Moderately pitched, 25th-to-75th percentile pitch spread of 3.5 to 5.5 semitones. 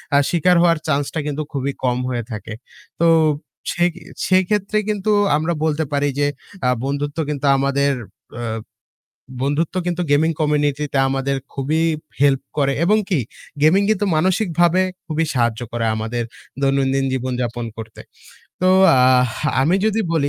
Yes: medium, 145 Hz; average, 4.1 semitones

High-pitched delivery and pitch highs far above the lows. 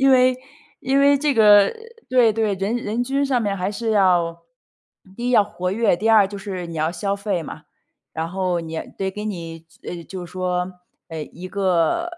No: high, 200 Hz; average, 4.4 semitones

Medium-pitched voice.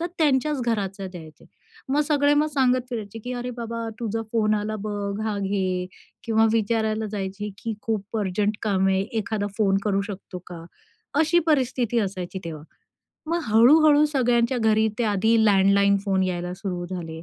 No: high, 215 Hz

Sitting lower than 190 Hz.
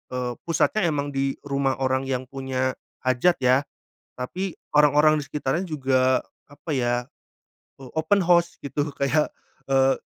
Yes: low, 135 Hz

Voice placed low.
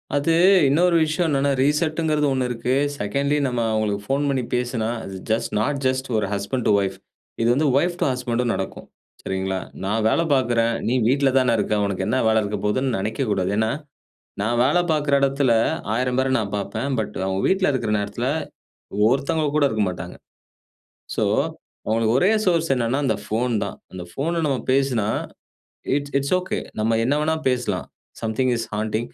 Yes: low, 125 Hz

